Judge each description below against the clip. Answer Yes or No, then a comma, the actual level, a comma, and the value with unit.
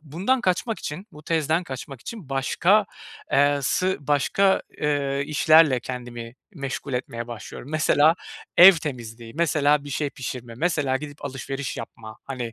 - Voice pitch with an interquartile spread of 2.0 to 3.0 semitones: No, average, 3.8 semitones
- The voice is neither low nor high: Yes, medium, 145 Hz